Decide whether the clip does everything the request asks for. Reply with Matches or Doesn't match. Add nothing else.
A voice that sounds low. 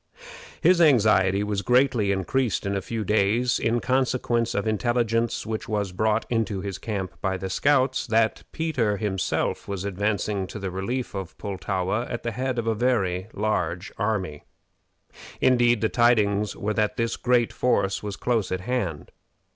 Matches